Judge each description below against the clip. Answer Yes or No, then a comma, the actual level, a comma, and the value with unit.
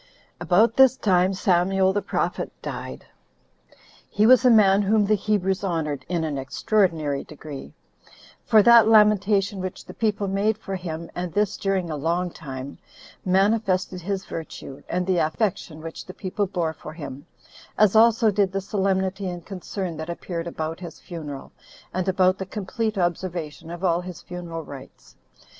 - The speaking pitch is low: No, medium, 185 Hz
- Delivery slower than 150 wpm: No, average, 160 wpm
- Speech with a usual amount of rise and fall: Yes, average, 3.4 semitones